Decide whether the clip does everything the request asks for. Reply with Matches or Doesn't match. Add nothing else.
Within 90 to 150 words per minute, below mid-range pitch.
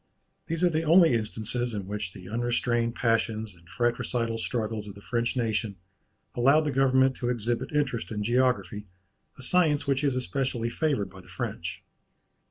Doesn't match